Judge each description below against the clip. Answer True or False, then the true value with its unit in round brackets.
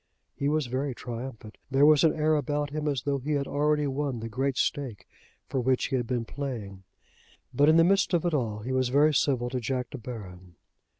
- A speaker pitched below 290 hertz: True (135 Hz)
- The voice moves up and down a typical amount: True (3.3 semitones)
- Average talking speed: False (220 wpm)